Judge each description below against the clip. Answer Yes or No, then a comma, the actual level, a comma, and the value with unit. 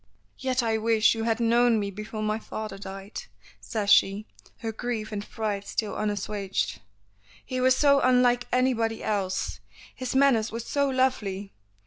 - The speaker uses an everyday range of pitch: Yes, average, 3.0 semitones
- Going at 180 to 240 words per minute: No, average, 150 wpm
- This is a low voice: No, high, 225 Hz